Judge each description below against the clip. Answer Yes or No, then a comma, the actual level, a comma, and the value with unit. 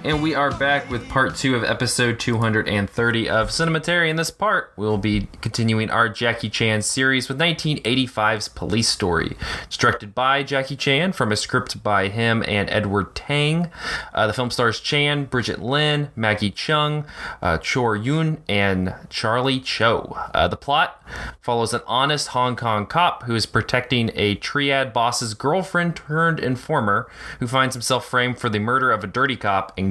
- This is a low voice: Yes, low, 125 Hz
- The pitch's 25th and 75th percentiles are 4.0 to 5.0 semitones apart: Yes, average, 4.7 semitones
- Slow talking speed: No, average, 170 wpm